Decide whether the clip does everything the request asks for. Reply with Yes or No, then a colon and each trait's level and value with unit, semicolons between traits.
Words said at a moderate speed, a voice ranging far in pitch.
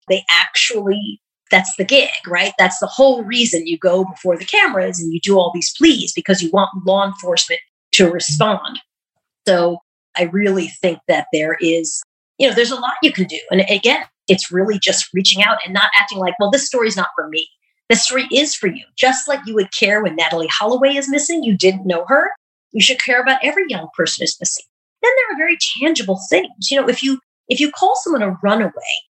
No: fast, 210 wpm; wide, 6.7 semitones